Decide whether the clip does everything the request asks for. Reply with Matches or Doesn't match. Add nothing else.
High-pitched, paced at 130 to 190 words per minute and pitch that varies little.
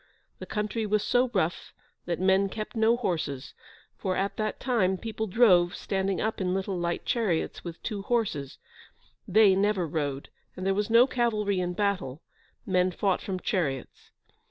Doesn't match